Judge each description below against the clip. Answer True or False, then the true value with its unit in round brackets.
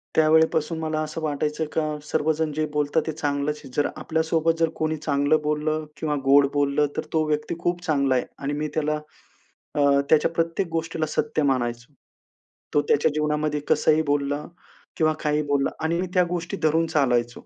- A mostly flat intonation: True (1.6 semitones)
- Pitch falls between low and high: True (155 Hz)